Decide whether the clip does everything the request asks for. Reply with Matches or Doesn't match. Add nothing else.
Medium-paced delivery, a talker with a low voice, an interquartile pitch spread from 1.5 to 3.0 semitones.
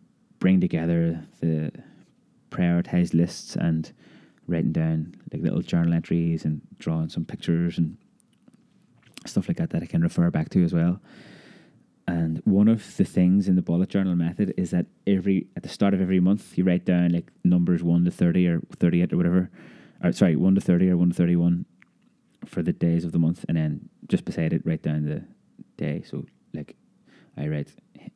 Matches